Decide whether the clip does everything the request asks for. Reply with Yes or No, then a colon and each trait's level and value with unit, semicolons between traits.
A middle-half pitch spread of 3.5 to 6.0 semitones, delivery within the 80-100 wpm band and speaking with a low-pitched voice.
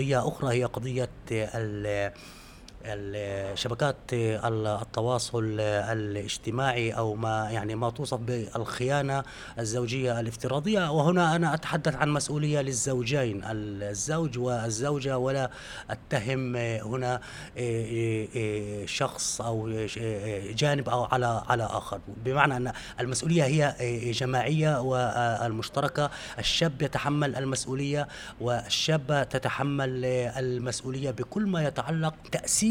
Yes: average, 3.8 semitones; average, 90 wpm; low, 125 Hz